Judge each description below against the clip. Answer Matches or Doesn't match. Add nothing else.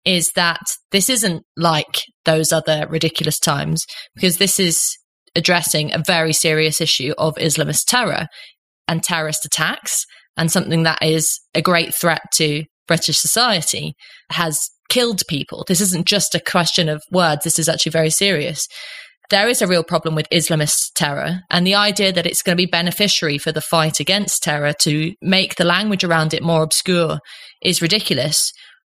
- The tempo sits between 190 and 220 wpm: Doesn't match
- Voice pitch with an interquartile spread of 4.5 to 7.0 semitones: Doesn't match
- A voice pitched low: Doesn't match